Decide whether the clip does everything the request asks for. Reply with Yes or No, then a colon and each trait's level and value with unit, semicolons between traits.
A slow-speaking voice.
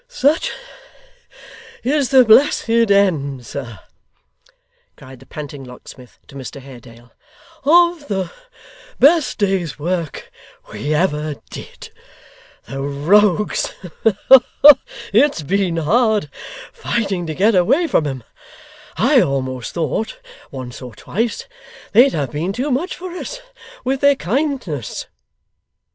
Yes: slow, 110 wpm